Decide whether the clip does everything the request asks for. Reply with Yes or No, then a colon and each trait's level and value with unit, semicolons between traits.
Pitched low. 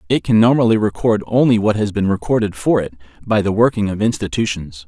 Yes: low, 110 Hz